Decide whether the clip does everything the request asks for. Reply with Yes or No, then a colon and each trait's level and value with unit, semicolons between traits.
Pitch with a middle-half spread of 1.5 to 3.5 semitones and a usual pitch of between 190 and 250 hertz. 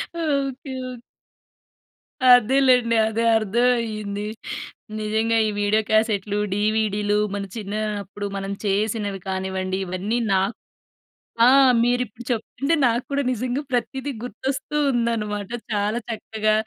Yes: average, 3.0 semitones; high, 220 Hz